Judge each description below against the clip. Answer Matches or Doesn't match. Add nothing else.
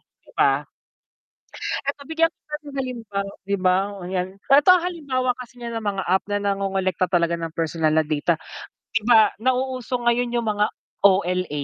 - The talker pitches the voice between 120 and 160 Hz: Doesn't match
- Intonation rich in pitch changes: Matches